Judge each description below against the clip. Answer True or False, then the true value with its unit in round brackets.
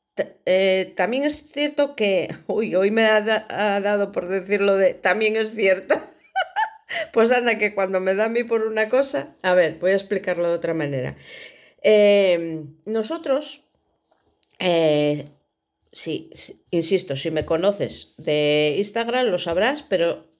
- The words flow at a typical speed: True (150 wpm)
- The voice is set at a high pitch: True (200 Hz)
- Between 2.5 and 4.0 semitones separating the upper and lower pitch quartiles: False (4.5 semitones)